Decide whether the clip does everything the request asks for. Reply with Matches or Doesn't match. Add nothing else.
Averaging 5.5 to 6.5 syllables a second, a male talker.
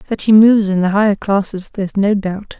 Doesn't match